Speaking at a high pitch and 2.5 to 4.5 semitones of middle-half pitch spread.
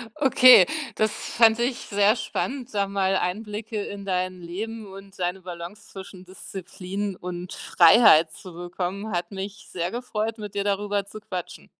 Yes: high, 200 Hz; average, 2.9 semitones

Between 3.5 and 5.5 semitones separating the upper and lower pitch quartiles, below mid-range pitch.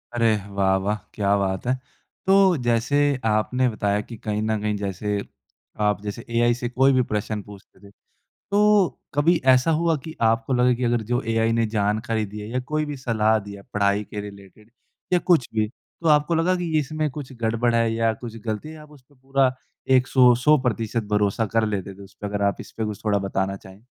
Yes: average, 4.0 semitones; low, 115 Hz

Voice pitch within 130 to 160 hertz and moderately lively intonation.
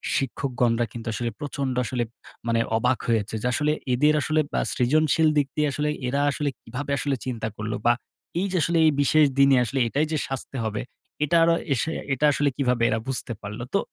Yes: low, 135 Hz; average, 3.9 semitones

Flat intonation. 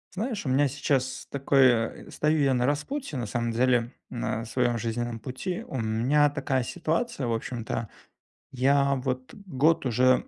No: average, 3.3 semitones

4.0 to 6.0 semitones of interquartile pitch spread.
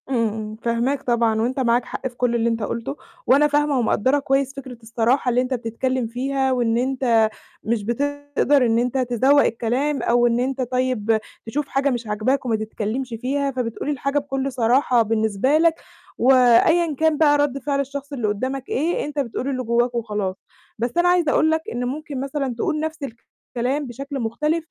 No: average, 3.2 semitones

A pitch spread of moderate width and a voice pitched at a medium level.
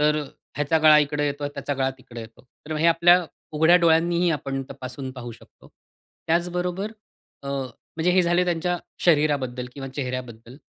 Yes: average, 4.4 semitones; medium, 150 Hz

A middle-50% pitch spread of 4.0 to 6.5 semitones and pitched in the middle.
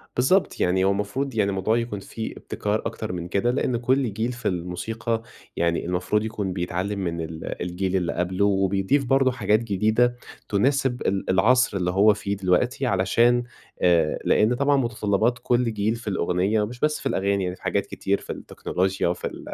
No: average, 4.3 semitones; low, 105 Hz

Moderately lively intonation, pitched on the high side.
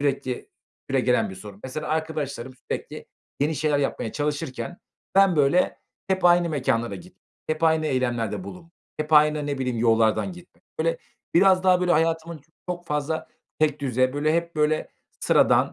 No: average, 3.8 semitones; medium, 155 Hz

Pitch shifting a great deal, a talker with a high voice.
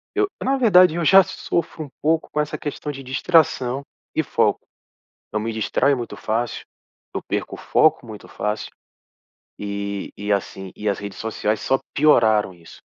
No: wide, 7.0 semitones; low, 125 Hz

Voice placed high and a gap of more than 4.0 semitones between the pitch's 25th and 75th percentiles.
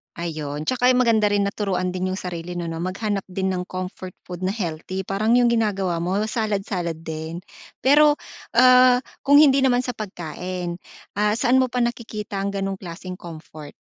Yes: high, 195 Hz; average, 4.7 semitones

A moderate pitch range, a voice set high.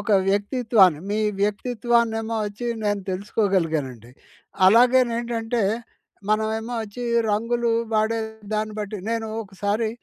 No: narrow, 2.3 semitones; high, 220 Hz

